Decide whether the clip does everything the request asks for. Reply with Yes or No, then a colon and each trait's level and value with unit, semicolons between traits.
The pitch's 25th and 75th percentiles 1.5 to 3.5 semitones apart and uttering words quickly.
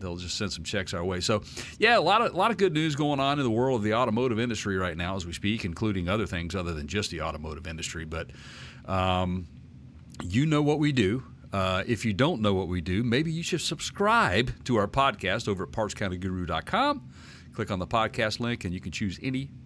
No: wide, 5.4 semitones; fast, 230 wpm